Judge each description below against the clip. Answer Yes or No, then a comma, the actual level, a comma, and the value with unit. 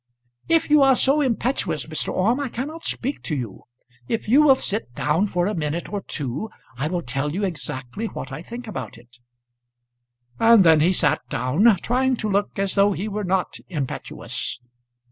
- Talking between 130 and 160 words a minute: No, average, 185 wpm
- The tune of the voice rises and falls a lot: Yes, wide, 7.6 semitones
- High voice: Yes, high, 195 Hz